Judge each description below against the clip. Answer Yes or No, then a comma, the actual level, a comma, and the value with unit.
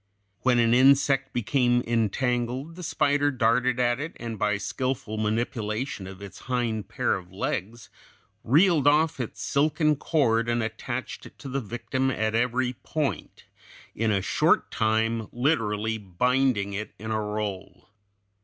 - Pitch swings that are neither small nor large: Yes, average, 3.5 semitones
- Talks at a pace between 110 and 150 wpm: Yes, average, 145 wpm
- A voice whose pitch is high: No, low, 120 Hz